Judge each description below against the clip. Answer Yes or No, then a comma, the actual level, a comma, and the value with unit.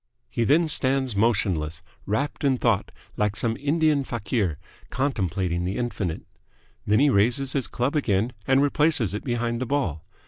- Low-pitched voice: Yes, low, 120 Hz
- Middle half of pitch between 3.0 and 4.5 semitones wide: No, wide, 5.5 semitones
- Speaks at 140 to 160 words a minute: Yes, average, 150 wpm